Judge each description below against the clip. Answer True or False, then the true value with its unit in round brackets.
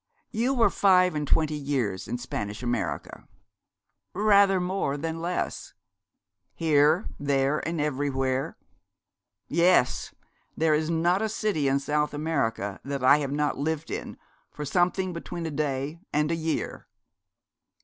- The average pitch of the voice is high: False (150 Hz)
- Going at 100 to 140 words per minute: True (135 wpm)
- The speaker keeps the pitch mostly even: False (3.7 semitones)